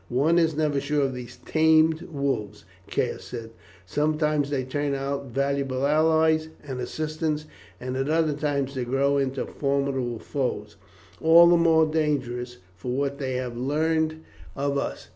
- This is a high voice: No, medium, 140 Hz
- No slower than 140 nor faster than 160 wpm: Yes, average, 145 wpm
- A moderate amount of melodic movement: Yes, average, 3.0 semitones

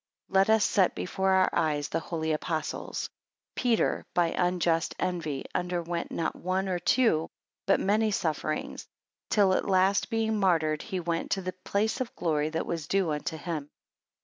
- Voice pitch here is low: No, medium, 180 Hz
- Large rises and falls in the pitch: No, average, 3.2 semitones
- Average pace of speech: Yes, average, 165 wpm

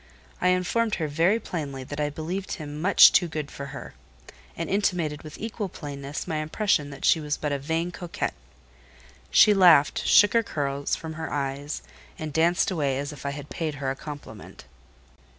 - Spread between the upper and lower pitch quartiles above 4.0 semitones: No, average, 3.7 semitones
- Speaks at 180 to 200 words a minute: Yes, average, 185 wpm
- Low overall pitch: No, medium, 155 Hz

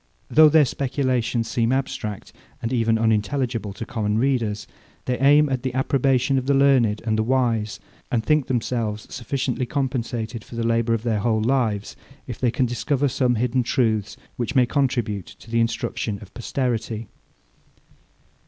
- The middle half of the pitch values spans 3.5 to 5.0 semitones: No, average, 2.9 semitones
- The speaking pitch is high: No, low, 120 Hz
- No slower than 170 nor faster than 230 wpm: No, average, 160 wpm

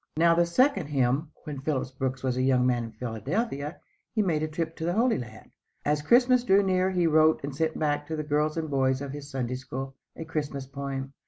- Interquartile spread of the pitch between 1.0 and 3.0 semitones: No, average, 3.8 semitones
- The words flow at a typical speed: No, fast, 225 wpm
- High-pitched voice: No, medium, 150 Hz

